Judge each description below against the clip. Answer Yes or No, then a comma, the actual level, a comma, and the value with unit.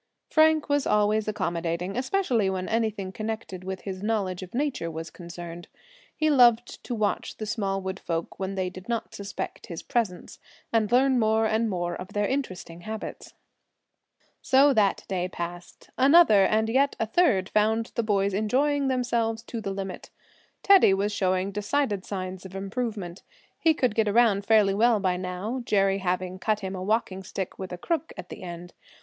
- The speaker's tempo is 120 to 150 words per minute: No, average, 175 wpm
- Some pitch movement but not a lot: Yes, average, 3.8 semitones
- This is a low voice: No, high, 205 Hz